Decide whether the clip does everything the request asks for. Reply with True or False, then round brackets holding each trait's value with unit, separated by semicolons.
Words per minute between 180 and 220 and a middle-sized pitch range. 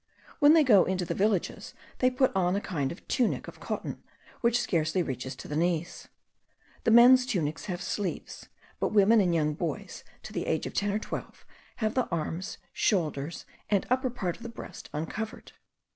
False (185 wpm; 5.7 semitones)